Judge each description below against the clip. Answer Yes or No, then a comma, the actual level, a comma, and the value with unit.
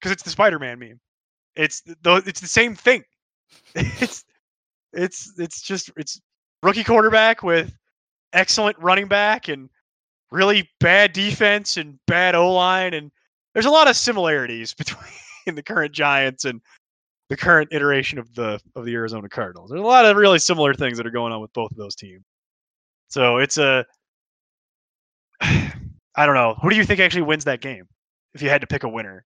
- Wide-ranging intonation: Yes, wide, 7.5 semitones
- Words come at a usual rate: Yes, average, 180 wpm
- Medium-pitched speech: Yes, medium, 155 Hz